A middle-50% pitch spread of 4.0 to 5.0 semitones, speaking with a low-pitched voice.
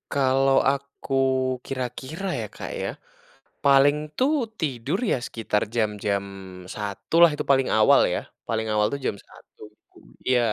Yes: average, 4.5 semitones; low, 130 Hz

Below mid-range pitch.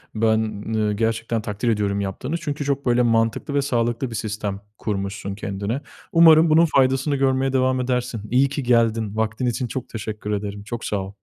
Yes: low, 115 Hz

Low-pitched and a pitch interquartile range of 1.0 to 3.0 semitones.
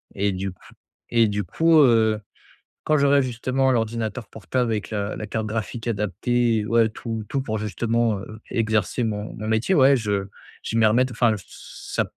Yes: low, 110 Hz; narrow, 2.4 semitones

